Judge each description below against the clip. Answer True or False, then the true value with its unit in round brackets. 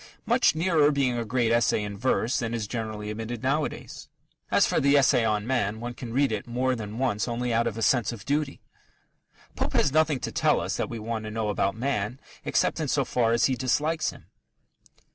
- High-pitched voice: False (120 Hz)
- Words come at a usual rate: False (215 wpm)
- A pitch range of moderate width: True (3.3 semitones)